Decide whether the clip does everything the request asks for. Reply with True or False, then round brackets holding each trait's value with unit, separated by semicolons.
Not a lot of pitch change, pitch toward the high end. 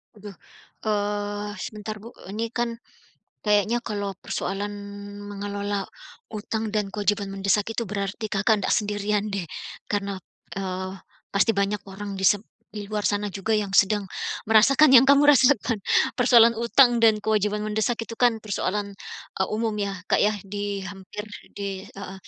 True (1.7 semitones; 210 Hz)